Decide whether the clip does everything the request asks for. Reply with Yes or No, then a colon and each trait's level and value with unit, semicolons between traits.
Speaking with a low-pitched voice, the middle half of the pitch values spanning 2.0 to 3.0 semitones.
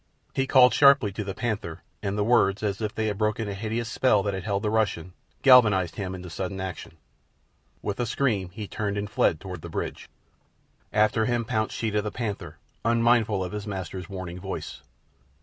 Yes: low, 105 Hz; average, 2.7 semitones